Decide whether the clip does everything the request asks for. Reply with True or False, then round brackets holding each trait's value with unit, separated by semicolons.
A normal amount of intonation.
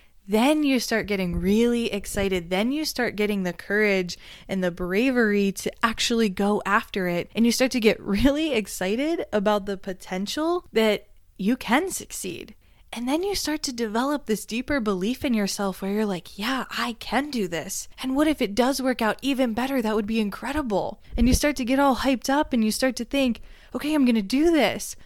True (4.6 semitones)